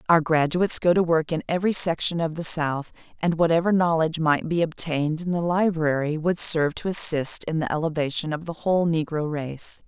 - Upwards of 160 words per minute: Yes, average, 195 wpm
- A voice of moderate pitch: Yes, medium, 165 Hz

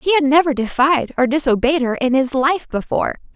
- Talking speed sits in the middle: Yes, average, 195 wpm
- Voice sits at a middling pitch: No, very high, 275 Hz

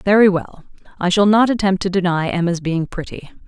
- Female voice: Yes, female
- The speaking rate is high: No, average, 190 wpm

